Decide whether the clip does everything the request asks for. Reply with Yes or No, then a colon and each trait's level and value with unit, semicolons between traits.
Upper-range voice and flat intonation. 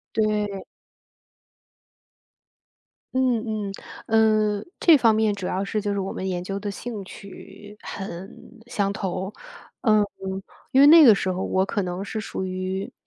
Yes: high, 205 Hz; narrow, 2.3 semitones